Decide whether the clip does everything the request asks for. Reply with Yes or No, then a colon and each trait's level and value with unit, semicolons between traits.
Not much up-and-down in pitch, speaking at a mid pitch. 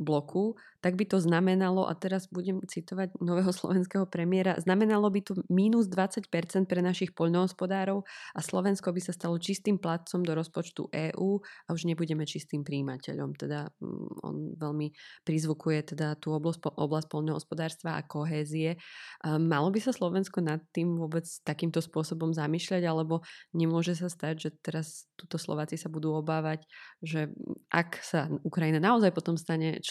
No: average, 3.0 semitones; medium, 165 Hz